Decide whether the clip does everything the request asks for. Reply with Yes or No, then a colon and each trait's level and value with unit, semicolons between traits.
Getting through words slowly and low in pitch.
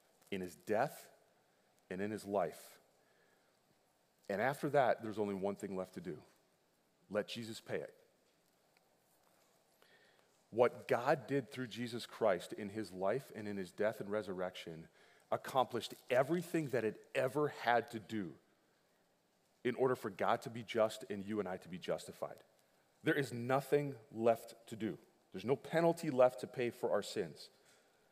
No: average, 155 wpm; low, 115 Hz